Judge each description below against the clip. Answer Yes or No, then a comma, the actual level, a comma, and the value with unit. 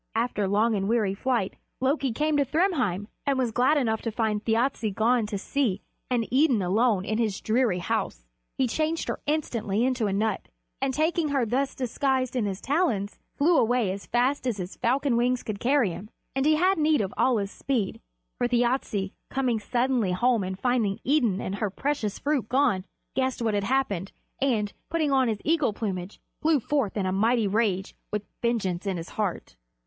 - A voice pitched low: No, high, 235 Hz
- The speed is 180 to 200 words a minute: Yes, average, 190 wpm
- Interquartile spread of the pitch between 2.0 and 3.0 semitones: No, average, 4.7 semitones